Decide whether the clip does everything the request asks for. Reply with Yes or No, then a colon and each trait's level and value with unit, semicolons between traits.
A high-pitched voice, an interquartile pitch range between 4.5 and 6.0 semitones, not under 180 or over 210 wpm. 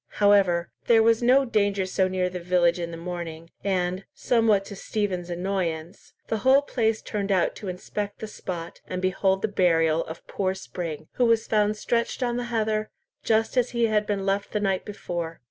No: high, 195 Hz; average, 3.5 semitones; average, 190 wpm